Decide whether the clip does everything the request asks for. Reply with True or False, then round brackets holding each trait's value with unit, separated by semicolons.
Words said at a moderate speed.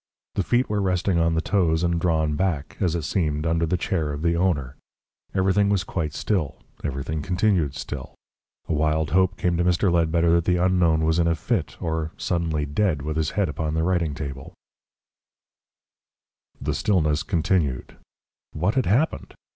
True (170 wpm)